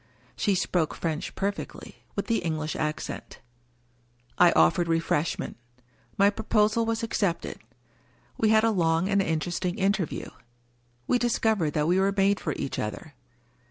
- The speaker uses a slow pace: No, average, 145 wpm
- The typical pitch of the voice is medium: Yes, medium, 180 Hz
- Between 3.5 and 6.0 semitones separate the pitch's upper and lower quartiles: Yes, average, 4.9 semitones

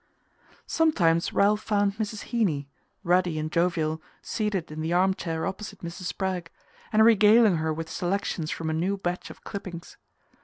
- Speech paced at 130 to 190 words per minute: Yes, average, 155 wpm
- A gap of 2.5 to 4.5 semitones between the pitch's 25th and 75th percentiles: Yes, average, 3.8 semitones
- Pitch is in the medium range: Yes, medium, 180 Hz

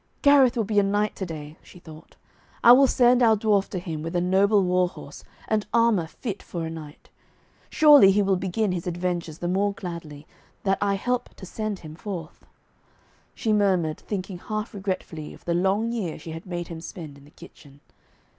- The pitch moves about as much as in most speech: Yes, average, 4.0 semitones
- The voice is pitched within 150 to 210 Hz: Yes, high, 190 Hz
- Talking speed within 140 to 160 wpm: No, average, 195 wpm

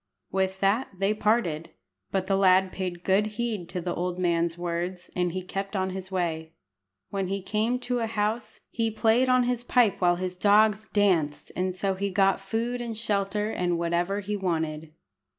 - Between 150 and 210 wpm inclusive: Yes, average, 180 wpm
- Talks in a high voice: Yes, high, 195 Hz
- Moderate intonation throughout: Yes, average, 3.2 semitones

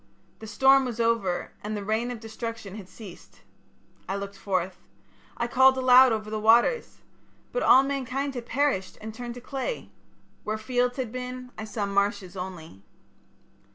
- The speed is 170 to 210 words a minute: No, average, 160 wpm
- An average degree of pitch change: Yes, average, 3.9 semitones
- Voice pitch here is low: No, high, 230 Hz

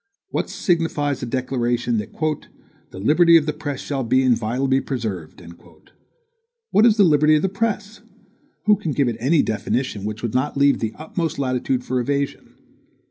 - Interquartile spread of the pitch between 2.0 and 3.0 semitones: No, average, 4.3 semitones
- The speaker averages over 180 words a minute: No, average, 165 wpm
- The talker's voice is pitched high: No, medium, 140 Hz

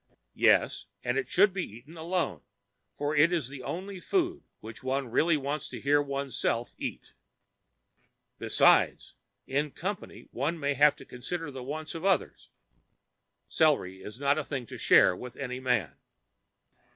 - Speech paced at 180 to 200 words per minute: No, average, 150 wpm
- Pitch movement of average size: Yes, average, 4.4 semitones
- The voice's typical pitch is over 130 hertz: Yes, medium, 140 Hz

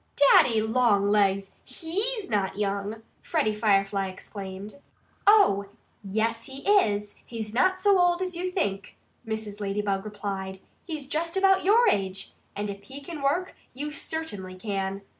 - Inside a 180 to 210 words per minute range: No, average, 140 wpm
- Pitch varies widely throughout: Yes, wide, 8.3 semitones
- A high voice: Yes, high, 215 Hz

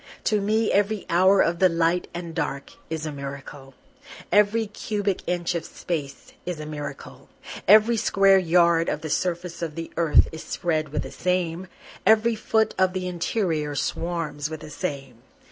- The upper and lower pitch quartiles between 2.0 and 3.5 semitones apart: No, average, 3.9 semitones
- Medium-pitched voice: Yes, medium, 170 Hz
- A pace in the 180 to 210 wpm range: No, average, 165 wpm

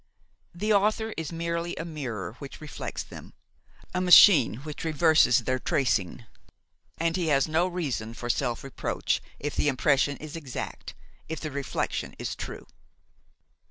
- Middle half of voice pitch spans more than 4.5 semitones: No, average, 4.1 semitones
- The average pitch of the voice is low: No, medium, 155 Hz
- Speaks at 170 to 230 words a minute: No, average, 145 wpm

